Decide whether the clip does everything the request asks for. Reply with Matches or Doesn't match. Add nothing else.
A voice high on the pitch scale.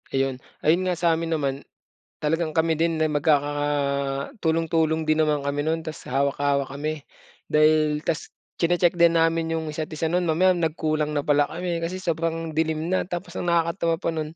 Doesn't match